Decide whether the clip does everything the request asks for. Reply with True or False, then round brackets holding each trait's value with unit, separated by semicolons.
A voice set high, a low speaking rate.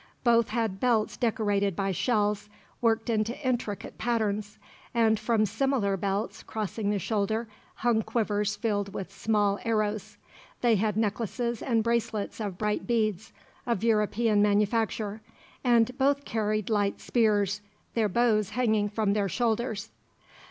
True (215 Hz; 130 wpm)